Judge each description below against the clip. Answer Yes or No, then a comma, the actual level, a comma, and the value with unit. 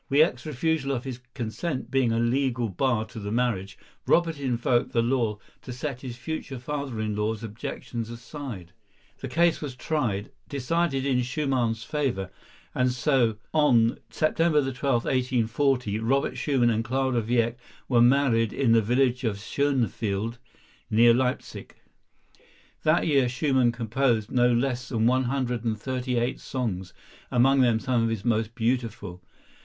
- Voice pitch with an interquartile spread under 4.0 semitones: Yes, average, 2.9 semitones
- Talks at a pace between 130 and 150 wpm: Yes, average, 145 wpm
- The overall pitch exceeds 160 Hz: No, low, 125 Hz